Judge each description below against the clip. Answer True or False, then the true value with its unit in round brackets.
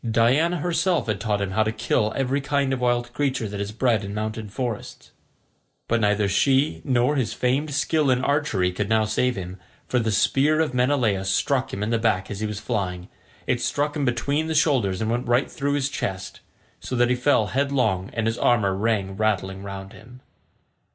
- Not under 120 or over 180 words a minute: False (200 wpm)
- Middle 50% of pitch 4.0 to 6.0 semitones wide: True (4.6 semitones)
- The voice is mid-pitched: False (120 Hz)